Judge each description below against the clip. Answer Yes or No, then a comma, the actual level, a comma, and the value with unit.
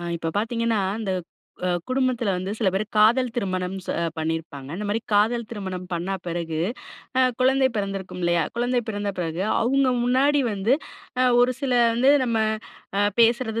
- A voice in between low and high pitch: No, high, 210 Hz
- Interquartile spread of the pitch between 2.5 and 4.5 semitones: No, average, 4.9 semitones